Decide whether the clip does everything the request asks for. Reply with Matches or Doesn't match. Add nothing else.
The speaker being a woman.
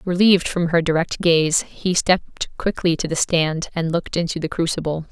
Matches